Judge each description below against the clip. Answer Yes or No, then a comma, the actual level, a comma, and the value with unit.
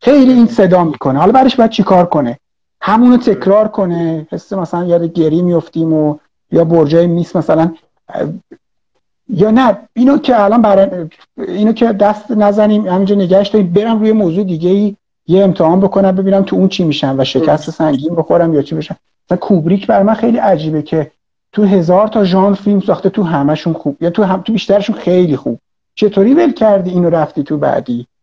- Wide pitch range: No, average, 4.1 semitones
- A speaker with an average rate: No, fast, 180 wpm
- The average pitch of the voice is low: No, high, 190 Hz